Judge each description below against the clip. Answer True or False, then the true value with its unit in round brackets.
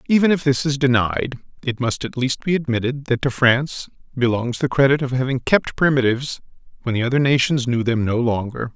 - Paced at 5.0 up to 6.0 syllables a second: True (5.7 syllables/s)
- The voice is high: False (130 Hz)